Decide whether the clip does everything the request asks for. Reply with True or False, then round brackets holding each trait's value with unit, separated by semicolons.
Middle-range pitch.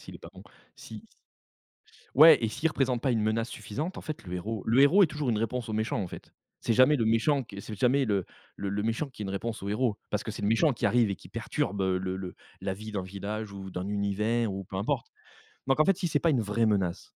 False (110 Hz)